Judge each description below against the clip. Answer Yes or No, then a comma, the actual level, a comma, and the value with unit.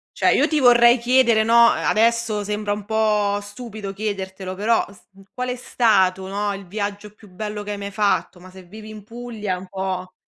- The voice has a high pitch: Yes, high, 210 Hz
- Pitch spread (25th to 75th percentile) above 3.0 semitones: No, narrow, 2.5 semitones